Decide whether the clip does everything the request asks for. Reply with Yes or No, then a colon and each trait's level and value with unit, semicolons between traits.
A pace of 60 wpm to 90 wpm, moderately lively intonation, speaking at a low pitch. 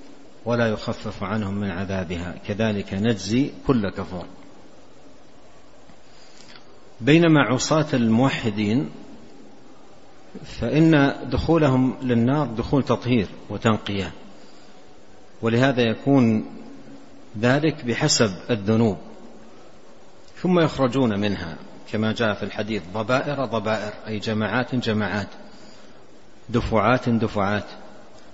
Yes: average, 80 wpm; average, 3.5 semitones; low, 115 Hz